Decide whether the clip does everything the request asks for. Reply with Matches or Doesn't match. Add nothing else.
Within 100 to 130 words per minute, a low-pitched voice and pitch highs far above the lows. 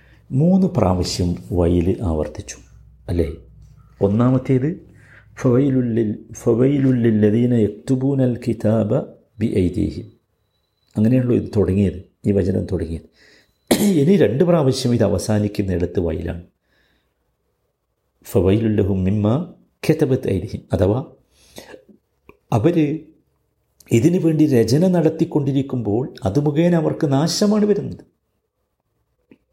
Doesn't match